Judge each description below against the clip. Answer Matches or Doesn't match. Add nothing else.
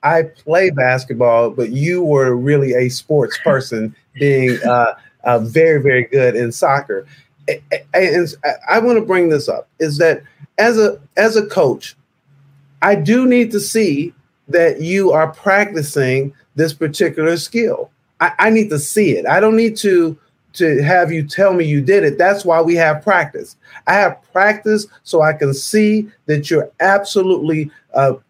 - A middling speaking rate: Matches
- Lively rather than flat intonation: Matches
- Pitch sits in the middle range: Matches